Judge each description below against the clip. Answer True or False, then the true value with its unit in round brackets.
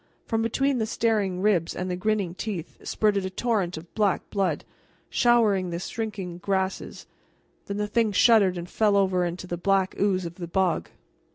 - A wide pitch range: False (3.0 semitones)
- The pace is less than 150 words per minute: False (175 wpm)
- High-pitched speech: True (195 Hz)